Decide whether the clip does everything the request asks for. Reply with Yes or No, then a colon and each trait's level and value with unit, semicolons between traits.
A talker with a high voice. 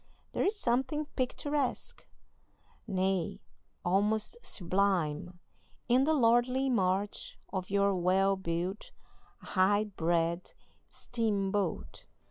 Yes: high, 200 Hz